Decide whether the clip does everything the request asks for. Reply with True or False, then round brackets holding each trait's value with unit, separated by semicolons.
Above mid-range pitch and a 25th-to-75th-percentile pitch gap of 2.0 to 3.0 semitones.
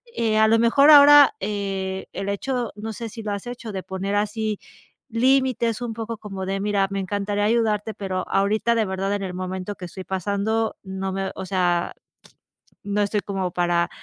True (205 Hz; 2.7 semitones)